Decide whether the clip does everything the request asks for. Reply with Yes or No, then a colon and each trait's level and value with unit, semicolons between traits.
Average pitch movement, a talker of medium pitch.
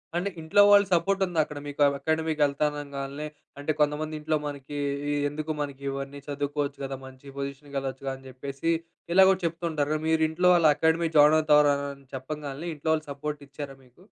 No: narrow, 2.3 semitones; medium, 150 Hz